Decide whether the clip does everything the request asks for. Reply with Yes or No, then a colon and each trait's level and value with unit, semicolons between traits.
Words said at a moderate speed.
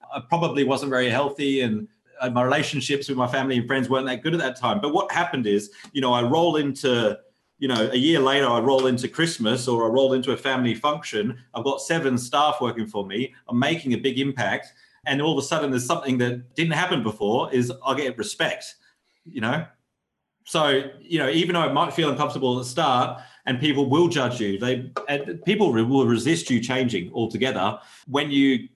No: fast, 210 wpm